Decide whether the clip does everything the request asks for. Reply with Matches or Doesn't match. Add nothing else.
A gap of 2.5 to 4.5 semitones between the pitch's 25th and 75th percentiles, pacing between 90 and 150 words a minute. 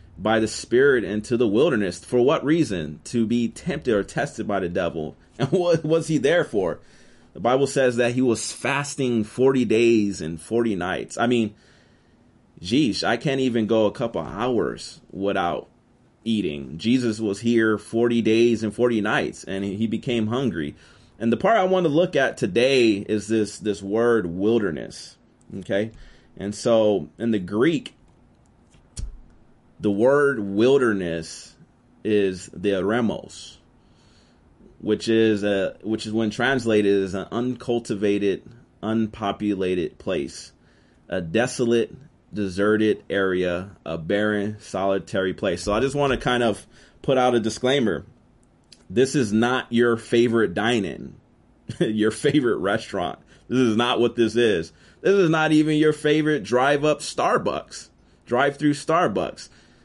Matches